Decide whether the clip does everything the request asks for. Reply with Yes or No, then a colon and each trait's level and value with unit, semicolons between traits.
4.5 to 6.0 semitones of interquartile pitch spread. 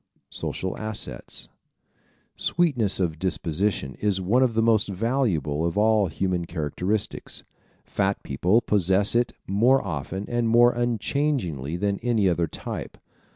Yes: average, 4.8 semitones